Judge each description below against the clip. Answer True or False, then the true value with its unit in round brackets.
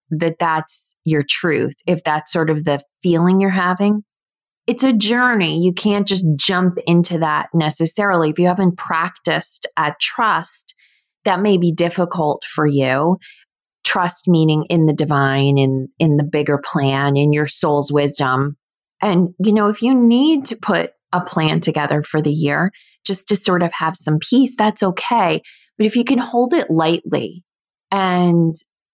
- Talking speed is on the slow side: False (165 wpm)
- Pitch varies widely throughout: False (4.3 semitones)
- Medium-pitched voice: True (170 Hz)